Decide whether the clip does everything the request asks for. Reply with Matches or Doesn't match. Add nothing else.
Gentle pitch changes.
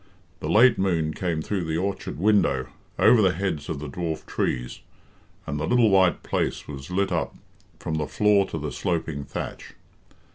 Doesn't match